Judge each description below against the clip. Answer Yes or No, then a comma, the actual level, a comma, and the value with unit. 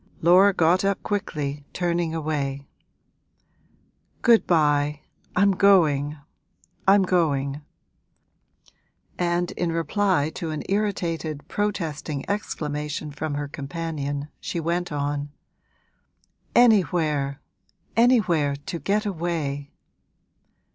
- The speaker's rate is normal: No, slow, 90 wpm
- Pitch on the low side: No, medium, 160 Hz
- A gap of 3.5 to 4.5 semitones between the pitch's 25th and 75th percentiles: Yes, average, 4.2 semitones